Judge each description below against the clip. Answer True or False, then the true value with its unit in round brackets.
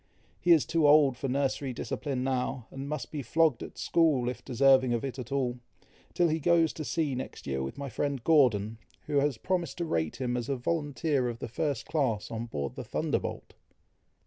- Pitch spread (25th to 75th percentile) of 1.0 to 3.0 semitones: False (3.8 semitones)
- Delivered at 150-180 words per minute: False (200 wpm)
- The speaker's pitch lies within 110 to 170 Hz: True (135 Hz)